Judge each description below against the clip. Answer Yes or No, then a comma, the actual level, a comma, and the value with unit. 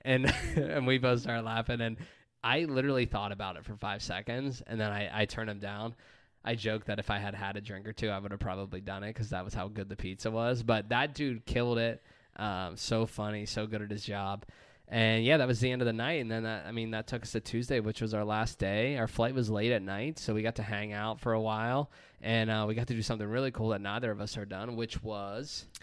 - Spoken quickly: Yes, fast, 270 wpm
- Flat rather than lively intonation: Yes, narrow, 2.2 semitones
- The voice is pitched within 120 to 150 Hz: No, low, 110 Hz